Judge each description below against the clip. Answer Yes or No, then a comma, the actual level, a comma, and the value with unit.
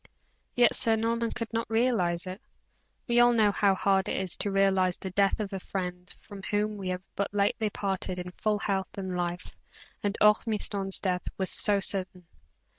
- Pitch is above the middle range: Yes, high, 195 Hz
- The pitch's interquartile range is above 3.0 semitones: No, narrow, 2.4 semitones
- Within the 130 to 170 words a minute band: No, average, 185 wpm